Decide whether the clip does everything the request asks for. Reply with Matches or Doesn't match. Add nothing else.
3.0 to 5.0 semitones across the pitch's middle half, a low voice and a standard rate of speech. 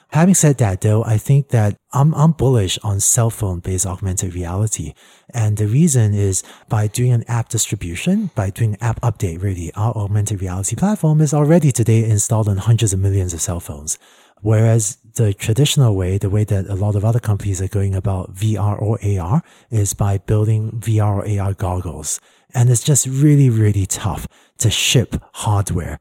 Matches